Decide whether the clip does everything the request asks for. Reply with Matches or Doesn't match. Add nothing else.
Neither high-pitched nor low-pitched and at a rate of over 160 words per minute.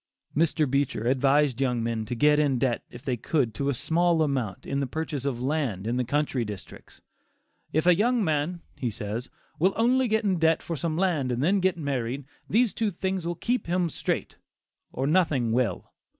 Matches